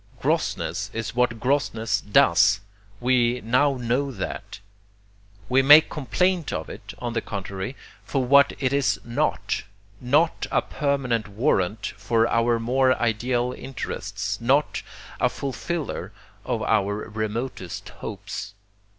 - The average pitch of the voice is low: Yes, low, 120 Hz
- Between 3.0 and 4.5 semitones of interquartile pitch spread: Yes, average, 4.0 semitones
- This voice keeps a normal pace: No, slow, 120 wpm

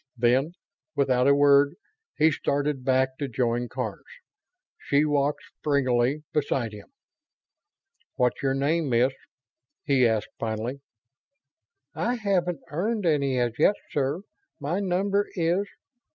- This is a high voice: No, medium, 140 Hz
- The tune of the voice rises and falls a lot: No, average, 4.0 semitones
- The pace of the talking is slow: Yes, slow, 120 wpm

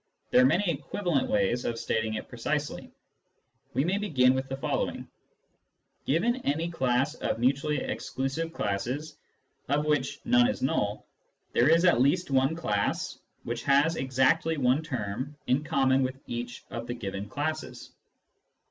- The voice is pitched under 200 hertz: Yes, low, 135 Hz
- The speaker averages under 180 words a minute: Yes, average, 155 wpm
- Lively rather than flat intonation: No, average, 4.5 semitones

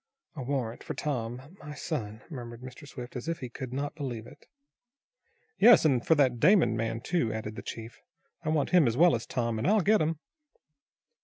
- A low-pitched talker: Yes, low, 130 Hz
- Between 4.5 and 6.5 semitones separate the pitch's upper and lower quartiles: Yes, average, 5.0 semitones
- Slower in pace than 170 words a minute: No, average, 200 wpm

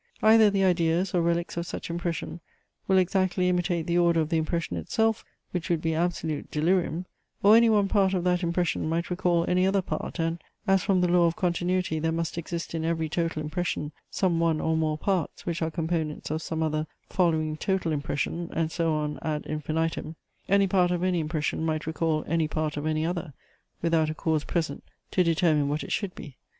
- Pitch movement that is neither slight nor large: No, narrow, 2.3 semitones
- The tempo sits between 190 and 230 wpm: Yes, average, 200 wpm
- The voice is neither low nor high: Yes, medium, 170 Hz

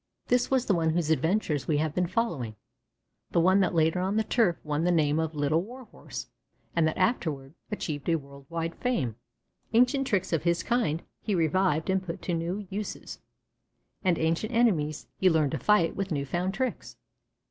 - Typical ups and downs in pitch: Yes, average, 4.2 semitones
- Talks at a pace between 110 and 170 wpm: No, average, 185 wpm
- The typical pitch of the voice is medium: Yes, medium, 170 Hz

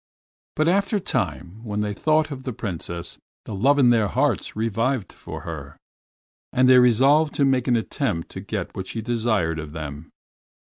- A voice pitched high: No, low, 115 Hz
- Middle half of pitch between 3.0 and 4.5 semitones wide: No, wide, 5.6 semitones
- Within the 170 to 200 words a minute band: Yes, average, 180 wpm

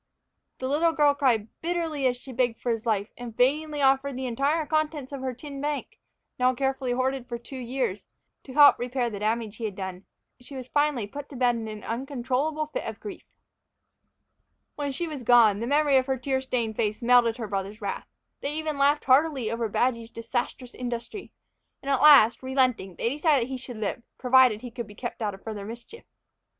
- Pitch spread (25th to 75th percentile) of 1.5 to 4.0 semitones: Yes, average, 3.5 semitones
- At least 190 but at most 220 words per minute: Yes, average, 200 wpm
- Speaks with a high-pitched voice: Yes, very high, 255 Hz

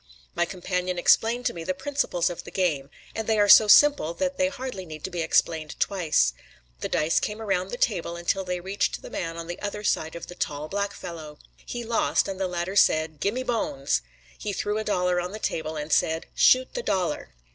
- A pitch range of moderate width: Yes, average, 4.1 semitones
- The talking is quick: Yes, fast, 220 wpm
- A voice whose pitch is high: No, medium, 180 Hz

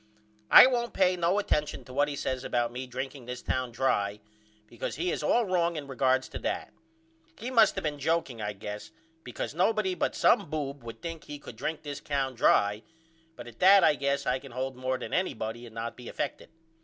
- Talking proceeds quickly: Yes, fast, 210 wpm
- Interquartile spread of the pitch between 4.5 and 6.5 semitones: Yes, wide, 5.5 semitones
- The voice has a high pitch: No, low, 135 Hz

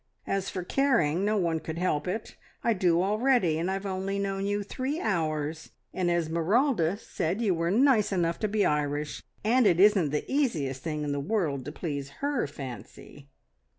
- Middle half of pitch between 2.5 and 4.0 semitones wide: No, average, 5.2 semitones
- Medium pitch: Yes, medium, 180 Hz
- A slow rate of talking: No, average, 180 wpm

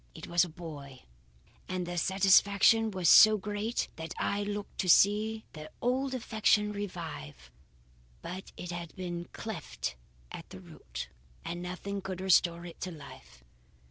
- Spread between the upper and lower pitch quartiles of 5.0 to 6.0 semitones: No, average, 3.4 semitones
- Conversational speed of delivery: Yes, average, 145 wpm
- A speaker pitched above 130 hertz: Yes, medium, 185 Hz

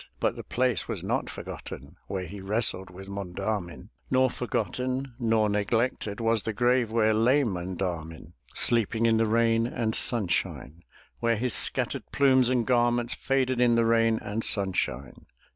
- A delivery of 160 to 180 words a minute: No, average, 150 wpm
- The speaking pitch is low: Yes, low, 115 Hz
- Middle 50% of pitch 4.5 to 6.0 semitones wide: No, average, 3.5 semitones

